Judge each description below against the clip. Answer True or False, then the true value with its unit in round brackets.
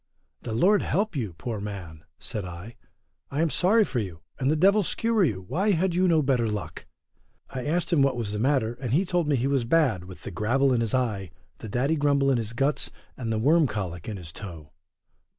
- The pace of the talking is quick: True (220 wpm)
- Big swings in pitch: True (7.1 semitones)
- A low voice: True (125 Hz)